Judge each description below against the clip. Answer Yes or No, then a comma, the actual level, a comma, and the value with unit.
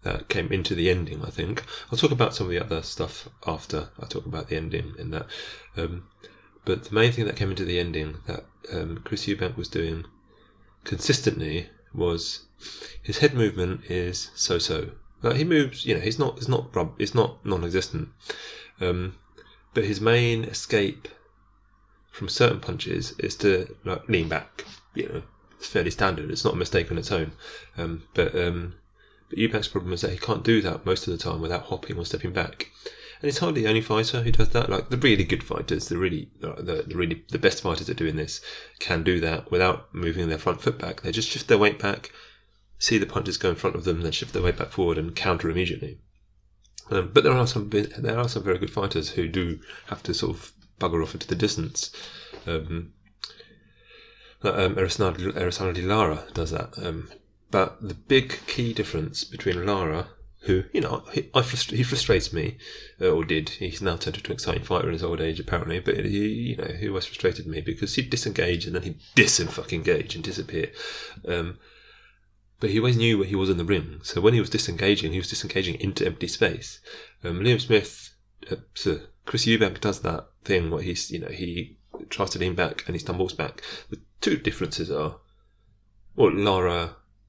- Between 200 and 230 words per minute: Yes, fast, 205 wpm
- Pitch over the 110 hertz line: No, very low, 95 Hz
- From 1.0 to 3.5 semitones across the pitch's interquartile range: No, average, 4.0 semitones